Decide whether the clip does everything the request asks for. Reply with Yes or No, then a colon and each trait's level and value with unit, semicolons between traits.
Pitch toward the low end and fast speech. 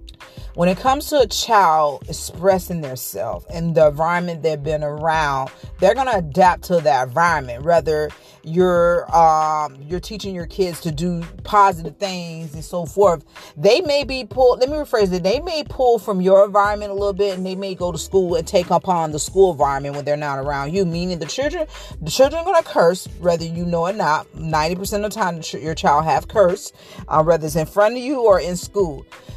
No: medium, 175 Hz; fast, 210 wpm